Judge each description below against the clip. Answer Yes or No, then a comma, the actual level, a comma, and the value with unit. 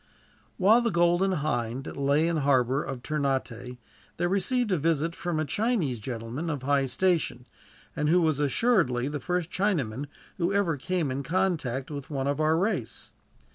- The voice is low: No, medium, 150 Hz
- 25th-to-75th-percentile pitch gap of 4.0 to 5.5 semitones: Yes, average, 5.1 semitones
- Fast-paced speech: No, average, 170 wpm